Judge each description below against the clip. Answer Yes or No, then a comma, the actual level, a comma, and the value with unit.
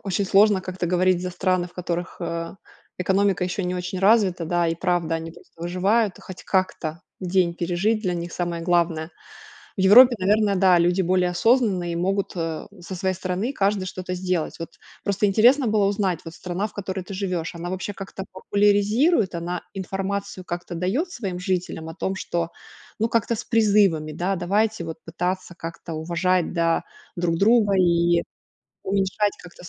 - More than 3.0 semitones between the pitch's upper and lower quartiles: No, narrow, 2.4 semitones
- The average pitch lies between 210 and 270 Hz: No, medium, 185 Hz